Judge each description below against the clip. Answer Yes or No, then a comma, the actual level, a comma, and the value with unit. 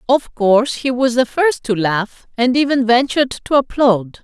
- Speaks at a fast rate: No, average, 185 wpm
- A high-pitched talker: Yes, high, 245 Hz